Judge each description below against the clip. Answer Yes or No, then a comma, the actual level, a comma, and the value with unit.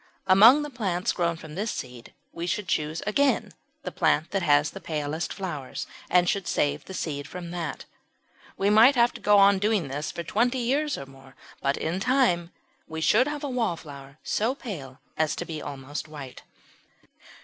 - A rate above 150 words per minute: Yes, average, 180 wpm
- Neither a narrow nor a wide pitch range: No, wide, 6.5 semitones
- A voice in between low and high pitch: Yes, medium, 175 Hz